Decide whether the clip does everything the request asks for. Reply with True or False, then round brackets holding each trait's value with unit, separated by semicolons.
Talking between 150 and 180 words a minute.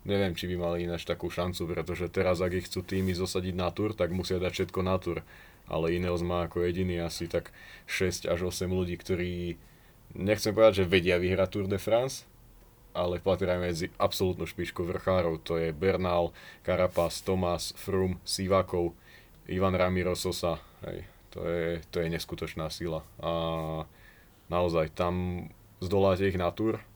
True (160 wpm)